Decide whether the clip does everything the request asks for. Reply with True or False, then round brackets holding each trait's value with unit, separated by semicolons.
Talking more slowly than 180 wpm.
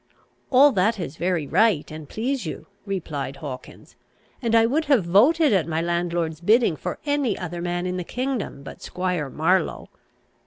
True (165 wpm)